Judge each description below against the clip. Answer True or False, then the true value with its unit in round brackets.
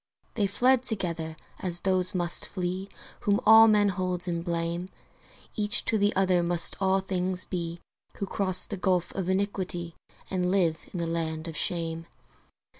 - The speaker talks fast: False (160 wpm)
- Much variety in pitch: False (2.4 semitones)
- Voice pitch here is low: False (185 Hz)